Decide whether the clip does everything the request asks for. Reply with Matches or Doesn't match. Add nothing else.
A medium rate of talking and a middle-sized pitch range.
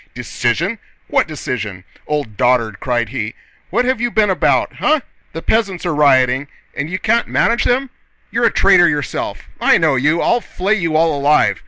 Doesn't match